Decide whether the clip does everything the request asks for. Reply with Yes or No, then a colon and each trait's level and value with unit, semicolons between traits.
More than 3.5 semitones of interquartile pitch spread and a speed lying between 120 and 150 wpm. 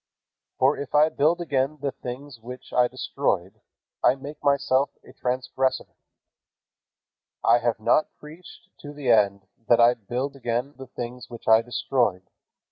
No: average, 3.1 semitones; average, 145 wpm